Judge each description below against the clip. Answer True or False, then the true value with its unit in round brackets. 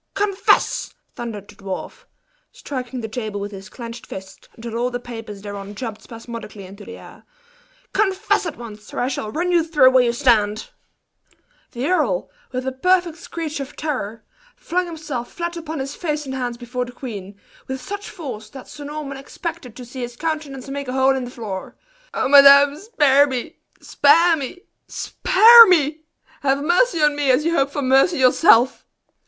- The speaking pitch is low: False (265 Hz)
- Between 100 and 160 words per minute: False (180 wpm)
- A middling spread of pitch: True (4.8 semitones)